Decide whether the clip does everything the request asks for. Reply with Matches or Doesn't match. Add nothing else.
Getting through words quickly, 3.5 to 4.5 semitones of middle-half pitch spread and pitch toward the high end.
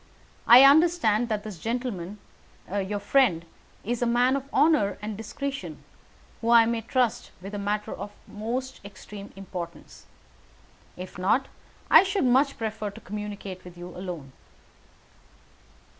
Doesn't match